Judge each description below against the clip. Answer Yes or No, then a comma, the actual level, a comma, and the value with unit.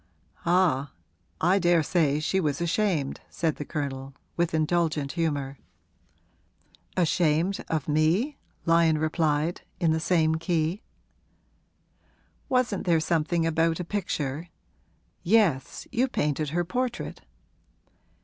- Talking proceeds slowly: Yes, slow, 105 wpm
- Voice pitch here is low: No, medium, 165 Hz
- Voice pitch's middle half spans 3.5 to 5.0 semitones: No, narrow, 2.6 semitones